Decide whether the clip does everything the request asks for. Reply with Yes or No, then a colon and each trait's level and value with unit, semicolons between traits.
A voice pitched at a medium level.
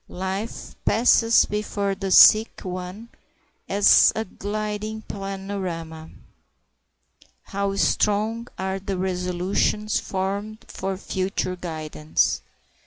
No: high, 195 Hz